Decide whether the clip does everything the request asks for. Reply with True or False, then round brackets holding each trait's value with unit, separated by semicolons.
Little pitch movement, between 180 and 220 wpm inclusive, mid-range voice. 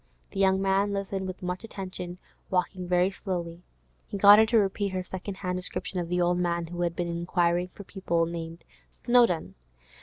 True (2.0 semitones; 185 wpm; 180 Hz)